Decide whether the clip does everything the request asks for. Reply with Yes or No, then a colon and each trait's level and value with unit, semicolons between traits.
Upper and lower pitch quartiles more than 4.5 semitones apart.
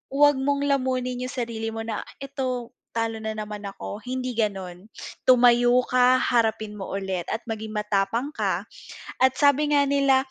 No: average, 3.2 semitones